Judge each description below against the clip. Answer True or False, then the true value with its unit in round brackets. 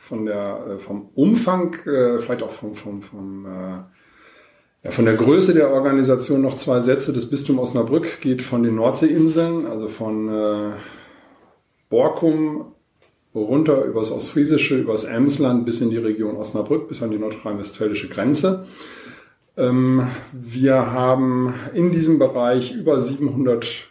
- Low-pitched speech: True (125 Hz)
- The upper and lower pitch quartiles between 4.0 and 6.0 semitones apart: True (4.5 semitones)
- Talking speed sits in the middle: True (135 wpm)